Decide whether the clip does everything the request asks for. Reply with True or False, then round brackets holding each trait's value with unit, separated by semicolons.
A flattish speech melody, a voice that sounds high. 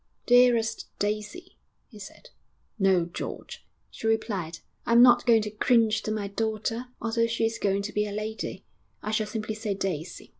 True (1.9 semitones; 215 Hz)